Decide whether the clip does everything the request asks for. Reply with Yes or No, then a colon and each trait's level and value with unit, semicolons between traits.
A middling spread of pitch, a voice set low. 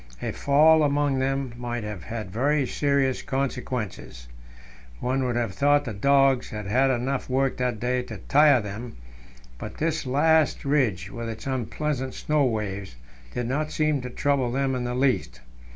Yes: average, 3.1 semitones; low, 130 Hz